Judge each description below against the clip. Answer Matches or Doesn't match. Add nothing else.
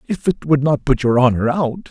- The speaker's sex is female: Doesn't match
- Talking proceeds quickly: Matches